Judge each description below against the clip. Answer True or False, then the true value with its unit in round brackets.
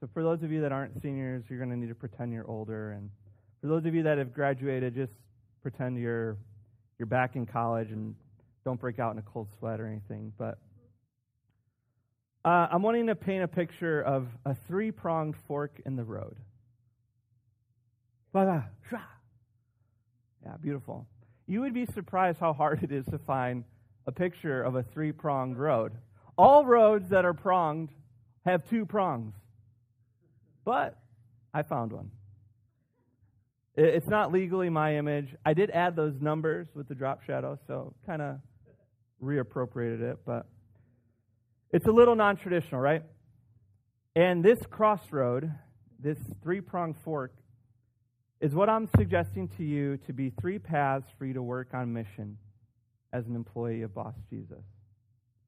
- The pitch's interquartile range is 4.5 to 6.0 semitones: True (5.0 semitones)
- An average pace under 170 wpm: True (155 wpm)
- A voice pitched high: False (125 Hz)